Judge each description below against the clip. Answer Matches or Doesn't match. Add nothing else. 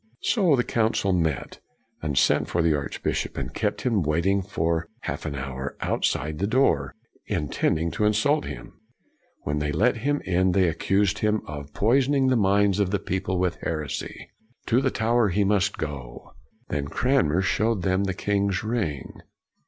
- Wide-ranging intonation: Matches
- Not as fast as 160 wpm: Doesn't match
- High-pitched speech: Doesn't match